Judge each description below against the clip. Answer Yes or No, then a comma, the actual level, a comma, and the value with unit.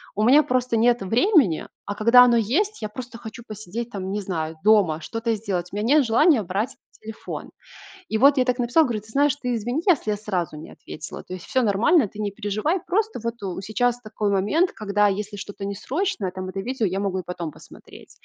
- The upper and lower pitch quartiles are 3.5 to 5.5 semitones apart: Yes, average, 3.9 semitones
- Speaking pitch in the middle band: No, high, 220 Hz